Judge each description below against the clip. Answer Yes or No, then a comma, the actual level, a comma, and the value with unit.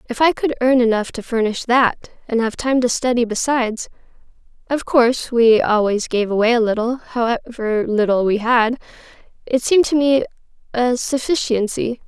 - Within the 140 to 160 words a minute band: Yes, average, 150 wpm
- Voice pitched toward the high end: Yes, high, 240 Hz